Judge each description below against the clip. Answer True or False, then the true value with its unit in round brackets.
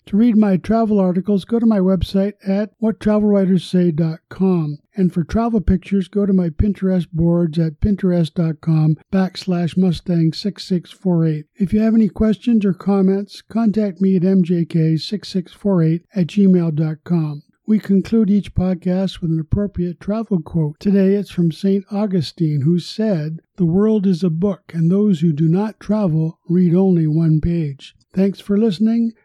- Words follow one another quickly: False (150 wpm)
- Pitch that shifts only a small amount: False (3.2 semitones)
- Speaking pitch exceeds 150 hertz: True (185 Hz)